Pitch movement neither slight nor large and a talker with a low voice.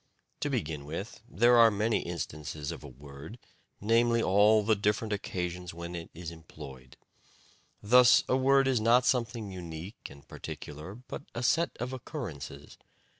No: wide, 6.6 semitones; low, 100 Hz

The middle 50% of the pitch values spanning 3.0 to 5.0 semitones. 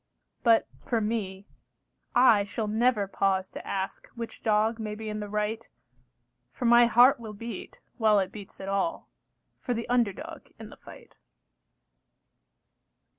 No: narrow, 2.5 semitones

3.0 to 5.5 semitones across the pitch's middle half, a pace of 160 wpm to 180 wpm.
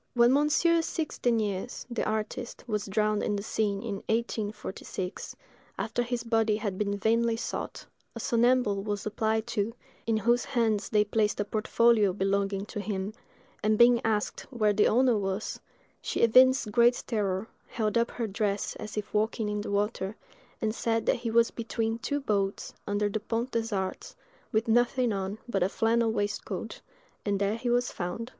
No: narrow, 2.4 semitones; average, 170 wpm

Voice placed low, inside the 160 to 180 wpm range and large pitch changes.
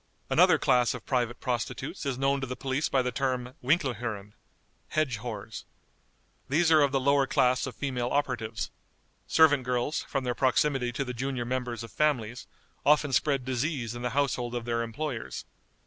No: low, 130 Hz; average, 175 wpm; narrow, 2.5 semitones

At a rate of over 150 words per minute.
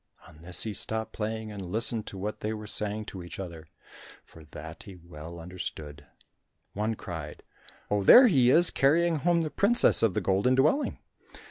Yes: average, 175 wpm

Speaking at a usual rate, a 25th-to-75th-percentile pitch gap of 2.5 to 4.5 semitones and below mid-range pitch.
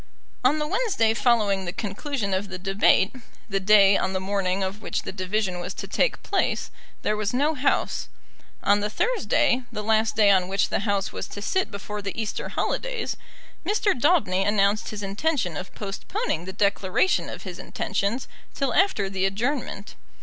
No: average, 175 wpm; average, 4.2 semitones; high, 205 Hz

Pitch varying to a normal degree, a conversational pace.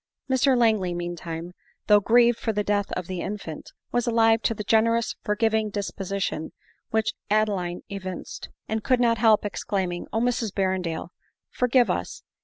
Yes: average, 3.5 semitones; average, 170 wpm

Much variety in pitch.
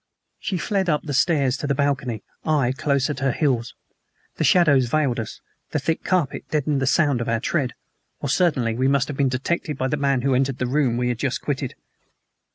No: average, 2.9 semitones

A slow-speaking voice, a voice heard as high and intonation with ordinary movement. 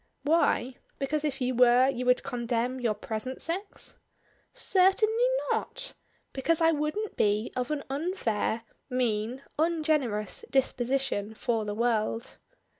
Yes: slow, 120 wpm; very high, 255 Hz; average, 4.8 semitones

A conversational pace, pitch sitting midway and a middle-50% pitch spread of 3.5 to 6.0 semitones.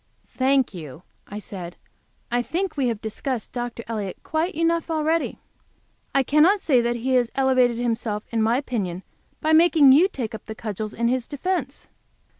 No: average, 170 wpm; high, 245 Hz; wide, 5.4 semitones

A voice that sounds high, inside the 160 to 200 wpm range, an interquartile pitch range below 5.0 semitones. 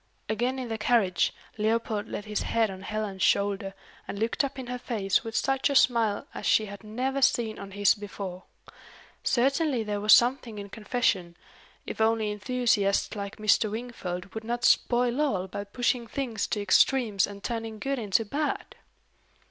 Yes: high, 220 Hz; average, 170 wpm; average, 3.3 semitones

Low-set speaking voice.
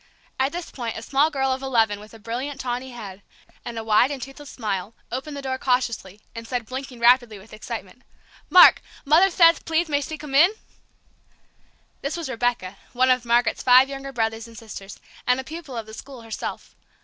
No: very high, 250 Hz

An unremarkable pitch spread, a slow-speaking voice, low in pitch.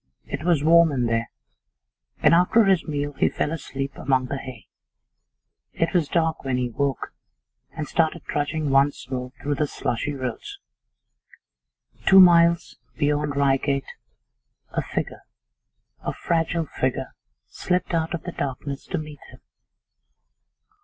No: average, 3.4 semitones; slow, 130 wpm; medium, 145 Hz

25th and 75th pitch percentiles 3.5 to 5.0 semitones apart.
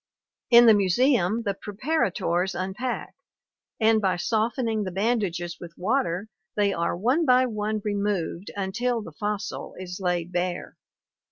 Yes: average, 4.1 semitones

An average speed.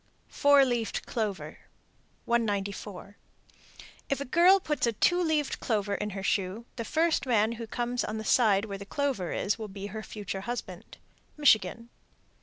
Yes: average, 165 wpm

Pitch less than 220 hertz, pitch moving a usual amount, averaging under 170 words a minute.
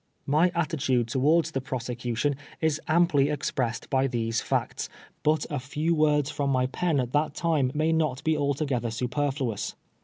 Yes: medium, 140 Hz; average, 3.4 semitones; average, 160 wpm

